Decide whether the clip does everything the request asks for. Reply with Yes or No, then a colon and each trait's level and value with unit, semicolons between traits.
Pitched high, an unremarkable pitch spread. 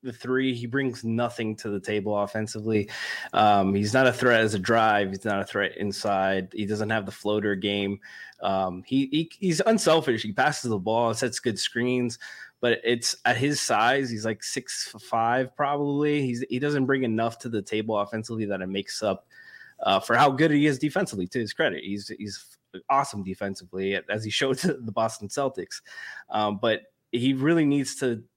No: low, 115 Hz; average, 4.3 semitones